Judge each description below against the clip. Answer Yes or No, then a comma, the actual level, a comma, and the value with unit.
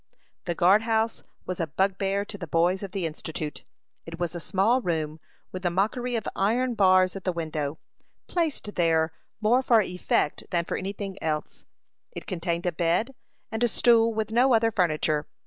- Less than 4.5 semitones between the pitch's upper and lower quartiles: No, average, 4.8 semitones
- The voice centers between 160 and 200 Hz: Yes, medium, 185 Hz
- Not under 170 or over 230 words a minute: Yes, average, 180 wpm